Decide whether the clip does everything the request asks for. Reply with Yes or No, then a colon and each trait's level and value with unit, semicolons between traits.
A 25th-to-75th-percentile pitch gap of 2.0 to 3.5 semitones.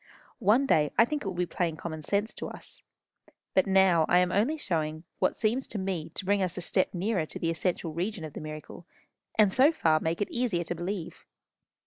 No: average, 3.9 semitones